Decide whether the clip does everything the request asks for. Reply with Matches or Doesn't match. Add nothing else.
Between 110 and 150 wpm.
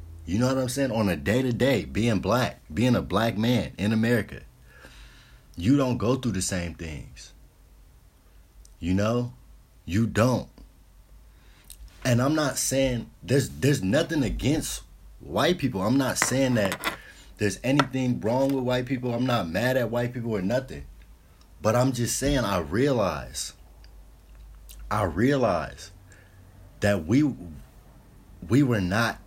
Matches